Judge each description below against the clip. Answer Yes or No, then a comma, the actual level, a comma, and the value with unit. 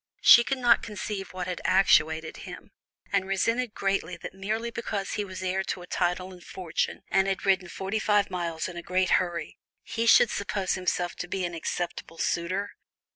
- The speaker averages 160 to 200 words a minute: Yes, average, 185 wpm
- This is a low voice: No, high, 190 Hz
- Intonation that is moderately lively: No, narrow, 2.2 semitones